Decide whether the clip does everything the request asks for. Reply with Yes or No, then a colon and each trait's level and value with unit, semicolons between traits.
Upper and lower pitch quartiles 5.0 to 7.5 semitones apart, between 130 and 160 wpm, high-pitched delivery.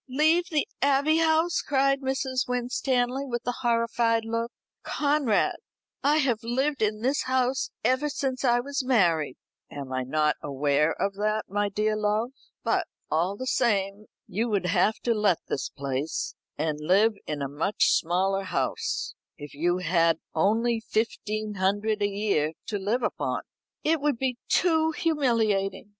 Yes: wide, 5.4 semitones; average, 150 wpm; high, 220 Hz